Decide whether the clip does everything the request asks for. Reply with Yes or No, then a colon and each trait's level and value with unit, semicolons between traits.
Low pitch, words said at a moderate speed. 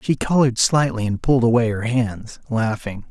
Yes: low, 120 Hz; average, 175 wpm